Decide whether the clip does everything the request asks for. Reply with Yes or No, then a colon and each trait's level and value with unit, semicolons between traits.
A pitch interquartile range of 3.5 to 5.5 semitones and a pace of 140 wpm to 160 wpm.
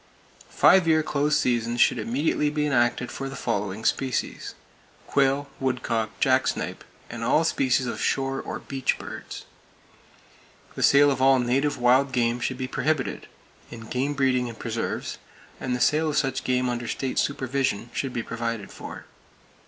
No: narrow, 2.5 semitones; average, 155 wpm